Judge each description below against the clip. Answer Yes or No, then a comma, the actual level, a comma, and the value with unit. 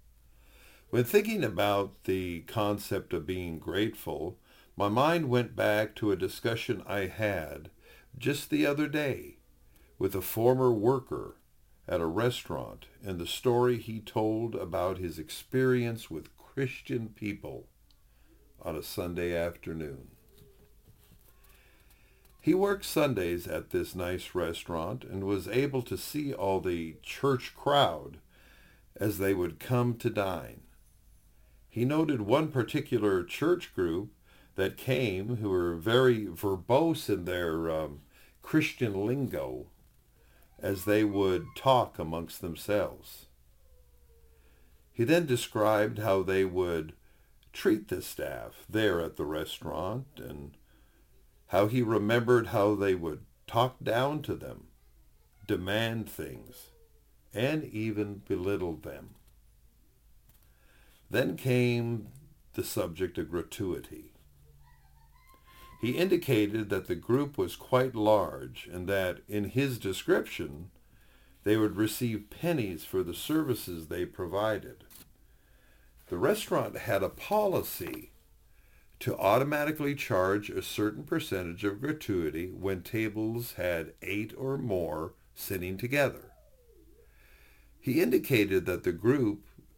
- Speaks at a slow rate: Yes, slow, 115 wpm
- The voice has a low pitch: Yes, low, 105 Hz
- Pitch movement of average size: No, wide, 6.0 semitones